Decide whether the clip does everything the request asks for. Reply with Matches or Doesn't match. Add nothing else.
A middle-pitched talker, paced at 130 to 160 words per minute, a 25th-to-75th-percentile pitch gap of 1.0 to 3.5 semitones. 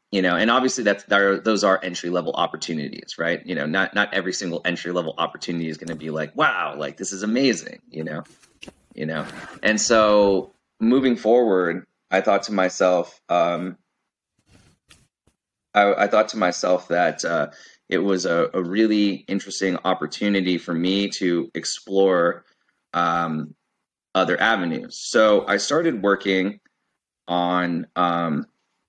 Doesn't match